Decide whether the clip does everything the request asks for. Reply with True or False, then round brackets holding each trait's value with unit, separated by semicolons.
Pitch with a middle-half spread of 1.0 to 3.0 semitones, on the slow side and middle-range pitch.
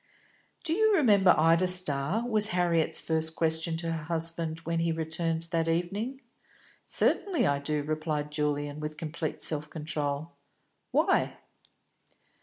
True (2.5 semitones; 130 wpm; 165 Hz)